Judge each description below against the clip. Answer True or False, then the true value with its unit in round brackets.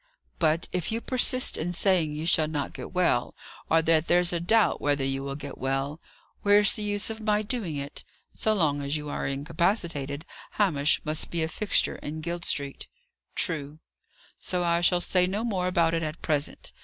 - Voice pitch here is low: False (165 Hz)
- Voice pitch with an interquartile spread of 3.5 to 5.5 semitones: True (4.1 semitones)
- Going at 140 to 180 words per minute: False (190 wpm)